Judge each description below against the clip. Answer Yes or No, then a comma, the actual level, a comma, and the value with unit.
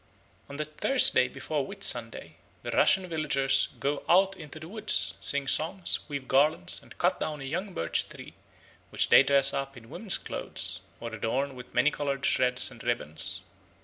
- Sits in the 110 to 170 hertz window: Yes, medium, 140 Hz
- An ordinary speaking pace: Yes, average, 170 wpm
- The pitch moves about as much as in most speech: Yes, average, 3.6 semitones